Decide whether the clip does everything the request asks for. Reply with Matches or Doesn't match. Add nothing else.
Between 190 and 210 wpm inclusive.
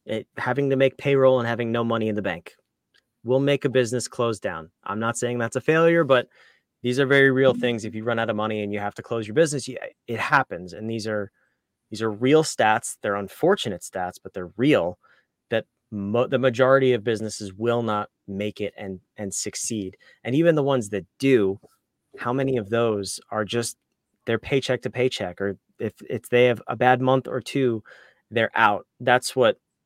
Matches